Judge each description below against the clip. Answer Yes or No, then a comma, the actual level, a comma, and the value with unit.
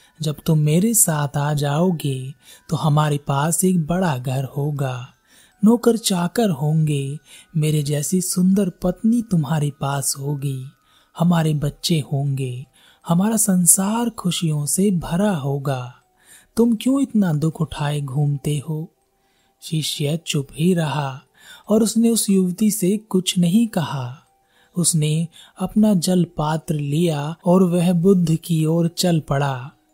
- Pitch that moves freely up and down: No, average, 4.2 semitones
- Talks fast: No, average, 125 wpm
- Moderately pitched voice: Yes, medium, 160 Hz